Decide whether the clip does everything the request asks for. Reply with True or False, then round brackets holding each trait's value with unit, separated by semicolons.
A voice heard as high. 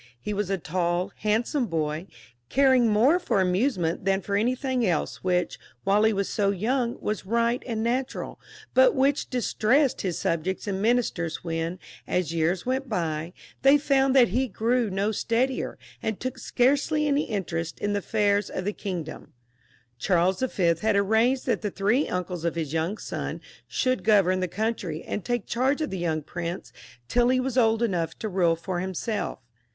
True (205 Hz)